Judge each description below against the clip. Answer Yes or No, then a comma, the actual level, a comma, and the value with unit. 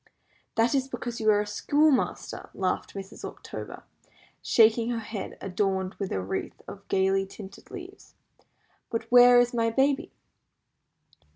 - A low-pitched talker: No, high, 225 Hz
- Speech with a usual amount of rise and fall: Yes, average, 4.0 semitones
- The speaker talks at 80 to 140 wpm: Yes, slow, 135 wpm